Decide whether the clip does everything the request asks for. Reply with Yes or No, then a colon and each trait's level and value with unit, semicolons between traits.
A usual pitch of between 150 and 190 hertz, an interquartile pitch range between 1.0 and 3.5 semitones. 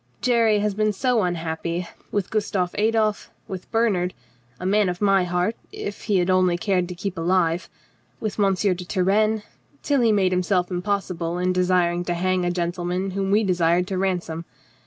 Yes: medium, 185 Hz; average, 2.7 semitones